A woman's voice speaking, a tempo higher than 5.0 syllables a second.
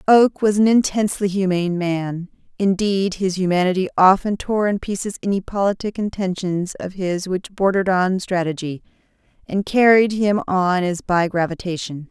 No: female; 4.9 syllables/s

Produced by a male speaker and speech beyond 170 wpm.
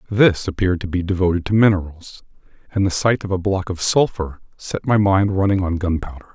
Yes: male; average, 200 wpm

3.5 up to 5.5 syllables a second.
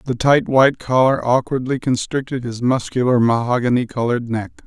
Yes: 5.4 syllables/s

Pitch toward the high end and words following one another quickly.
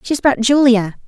No: high, 245 Hz; average, 170 wpm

